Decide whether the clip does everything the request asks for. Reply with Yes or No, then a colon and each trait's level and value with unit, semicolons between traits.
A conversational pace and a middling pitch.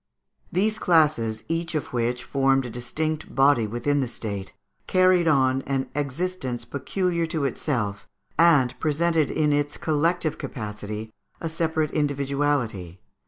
No: slow, 130 wpm; medium, 145 Hz